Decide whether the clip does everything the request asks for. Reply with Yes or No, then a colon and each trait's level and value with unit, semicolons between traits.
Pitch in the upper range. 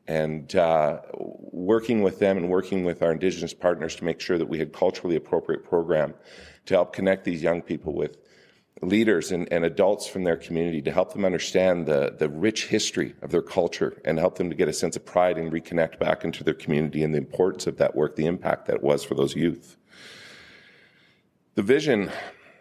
No: very low, 85 Hz